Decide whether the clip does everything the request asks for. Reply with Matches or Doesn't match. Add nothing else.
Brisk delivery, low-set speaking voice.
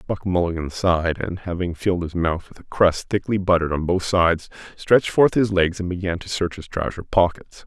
Matches